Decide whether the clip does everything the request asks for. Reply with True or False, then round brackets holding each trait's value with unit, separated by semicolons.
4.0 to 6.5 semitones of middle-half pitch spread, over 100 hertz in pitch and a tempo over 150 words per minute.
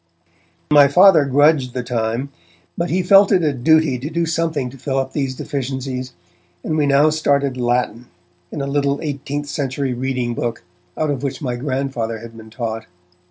False (2.9 semitones; 135 Hz; 175 wpm)